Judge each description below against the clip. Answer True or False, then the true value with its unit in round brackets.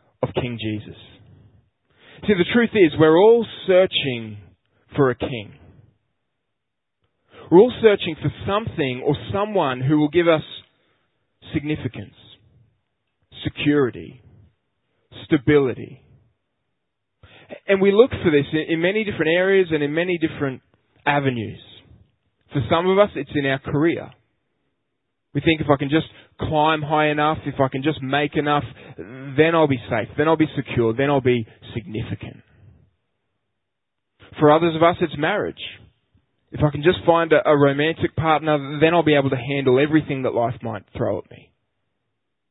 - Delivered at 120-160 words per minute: True (145 wpm)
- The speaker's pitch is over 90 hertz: True (140 Hz)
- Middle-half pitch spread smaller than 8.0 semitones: True (5.1 semitones)